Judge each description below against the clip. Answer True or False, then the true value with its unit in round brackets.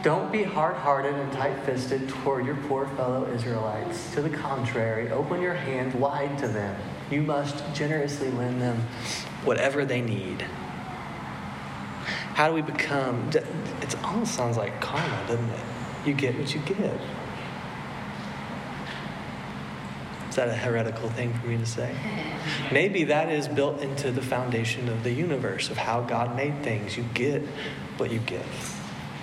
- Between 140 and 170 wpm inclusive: True (150 wpm)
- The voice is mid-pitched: False (125 Hz)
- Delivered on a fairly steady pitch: False (3.7 semitones)